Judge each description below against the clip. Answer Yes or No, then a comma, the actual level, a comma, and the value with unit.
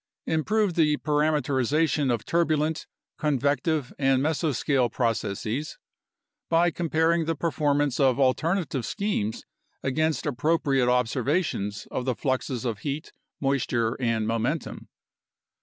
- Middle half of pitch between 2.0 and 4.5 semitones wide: Yes, average, 4.1 semitones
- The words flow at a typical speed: No, slow, 105 wpm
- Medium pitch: Yes, medium, 145 Hz